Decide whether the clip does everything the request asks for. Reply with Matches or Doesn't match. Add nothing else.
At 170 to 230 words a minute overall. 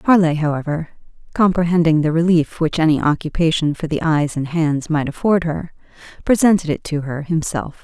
Doesn't match